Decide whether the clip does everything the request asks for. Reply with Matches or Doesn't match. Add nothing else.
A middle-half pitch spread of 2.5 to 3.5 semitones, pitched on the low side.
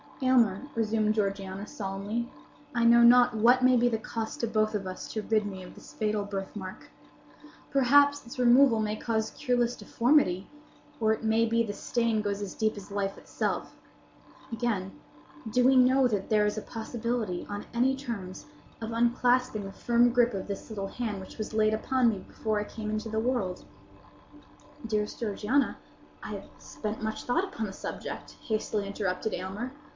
Doesn't match